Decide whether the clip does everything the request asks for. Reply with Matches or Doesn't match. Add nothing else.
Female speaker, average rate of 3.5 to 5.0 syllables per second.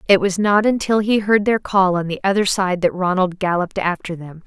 Doesn't match